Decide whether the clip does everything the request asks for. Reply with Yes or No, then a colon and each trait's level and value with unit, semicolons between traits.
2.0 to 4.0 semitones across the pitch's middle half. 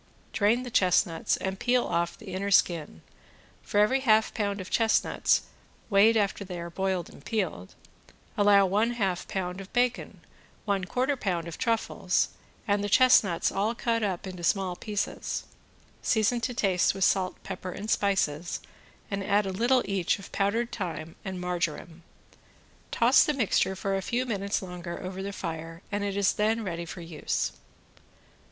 Yes: average, 3.4 semitones